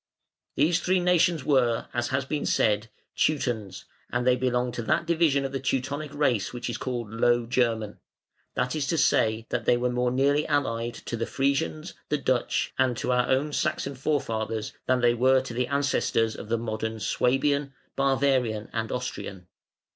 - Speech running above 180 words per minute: No, average, 175 wpm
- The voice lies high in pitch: No, low, 125 Hz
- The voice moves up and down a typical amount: Yes, average, 3.2 semitones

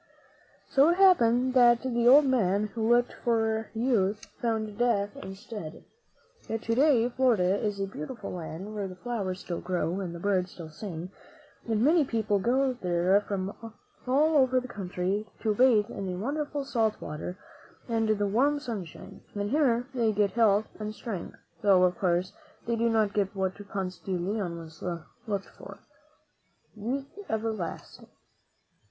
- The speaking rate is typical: Yes, average, 160 wpm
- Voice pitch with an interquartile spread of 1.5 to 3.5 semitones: No, average, 4.1 semitones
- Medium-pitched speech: No, high, 215 Hz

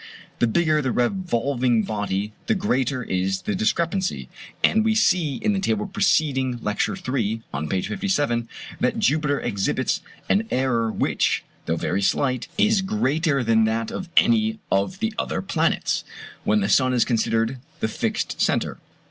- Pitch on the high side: No, low, 130 Hz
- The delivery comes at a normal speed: Yes, average, 155 wpm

